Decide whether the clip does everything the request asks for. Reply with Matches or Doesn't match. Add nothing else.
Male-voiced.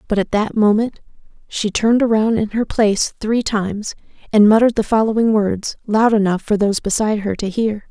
Doesn't match